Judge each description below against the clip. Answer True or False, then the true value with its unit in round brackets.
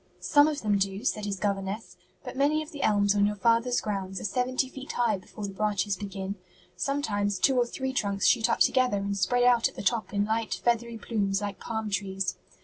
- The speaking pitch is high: True (210 Hz)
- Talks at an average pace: False (215 wpm)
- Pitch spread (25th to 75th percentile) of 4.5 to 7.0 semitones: False (3.5 semitones)